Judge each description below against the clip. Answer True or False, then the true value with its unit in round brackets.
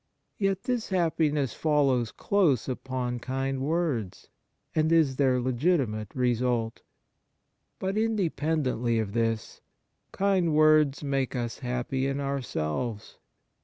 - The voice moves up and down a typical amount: True (4.6 semitones)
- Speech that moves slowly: True (105 wpm)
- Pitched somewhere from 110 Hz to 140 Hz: True (135 Hz)